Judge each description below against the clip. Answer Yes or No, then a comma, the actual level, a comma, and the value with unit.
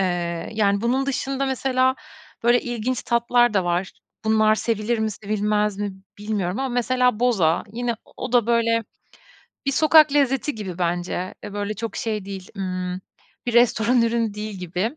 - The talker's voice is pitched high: Yes, high, 220 Hz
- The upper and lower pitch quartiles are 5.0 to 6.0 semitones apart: No, average, 3.6 semitones